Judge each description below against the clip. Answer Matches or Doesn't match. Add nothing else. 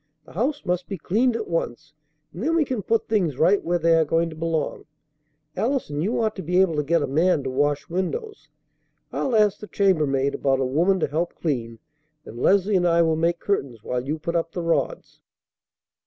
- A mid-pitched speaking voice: Matches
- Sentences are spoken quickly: Matches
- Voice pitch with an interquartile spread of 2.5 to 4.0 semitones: Doesn't match